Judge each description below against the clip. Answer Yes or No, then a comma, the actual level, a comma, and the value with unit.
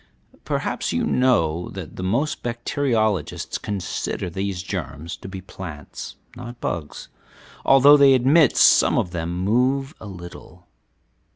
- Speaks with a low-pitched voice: Yes, low, 100 Hz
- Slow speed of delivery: Yes, slow, 120 wpm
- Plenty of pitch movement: Yes, wide, 6.4 semitones